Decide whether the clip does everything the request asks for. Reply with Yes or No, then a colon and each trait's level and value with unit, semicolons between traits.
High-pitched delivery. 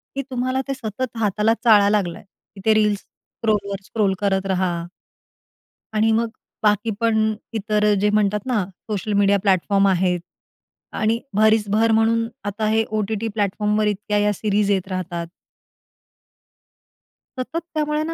Yes: high, 210 Hz